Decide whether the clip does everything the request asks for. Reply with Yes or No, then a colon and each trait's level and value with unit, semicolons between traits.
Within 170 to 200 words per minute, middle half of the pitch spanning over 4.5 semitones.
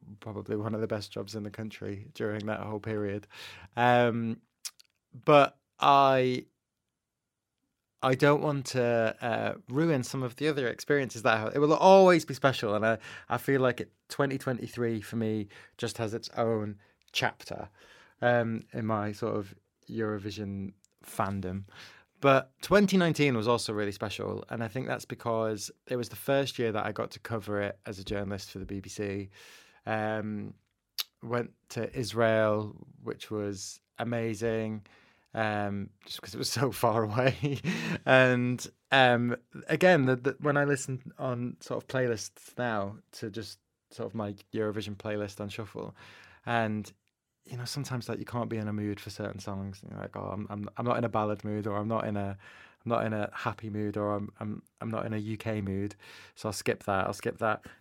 No: average, 180 wpm; average, 3.0 semitones